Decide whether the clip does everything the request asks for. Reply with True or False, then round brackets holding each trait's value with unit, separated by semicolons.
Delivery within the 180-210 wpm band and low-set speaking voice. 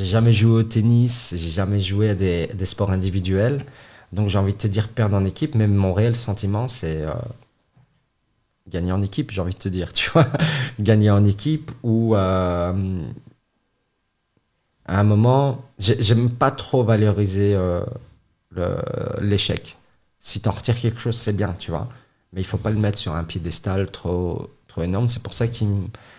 True (185 wpm; 105 Hz)